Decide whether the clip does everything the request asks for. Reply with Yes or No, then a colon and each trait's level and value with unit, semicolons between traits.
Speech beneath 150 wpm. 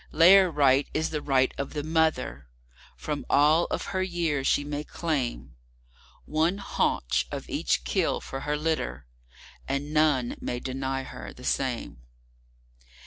Yes: average, 140 wpm